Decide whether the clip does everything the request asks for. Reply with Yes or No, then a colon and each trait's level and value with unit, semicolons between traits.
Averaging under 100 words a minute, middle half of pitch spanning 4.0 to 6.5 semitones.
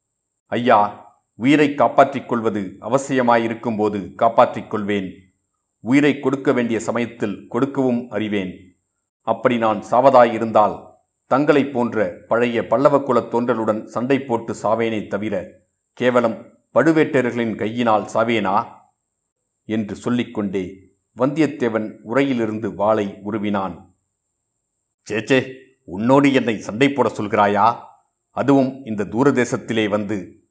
No: average, 90 wpm; average, 3.6 semitones